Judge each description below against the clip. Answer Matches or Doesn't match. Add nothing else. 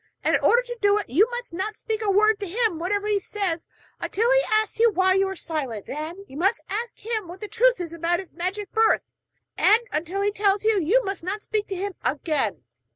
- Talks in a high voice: Matches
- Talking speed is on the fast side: Matches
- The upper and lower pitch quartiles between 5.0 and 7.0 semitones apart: Doesn't match